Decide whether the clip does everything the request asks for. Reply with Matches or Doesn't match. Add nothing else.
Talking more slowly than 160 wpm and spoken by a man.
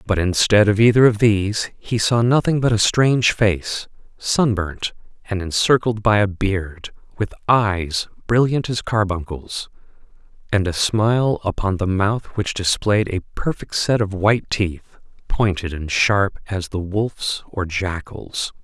Matches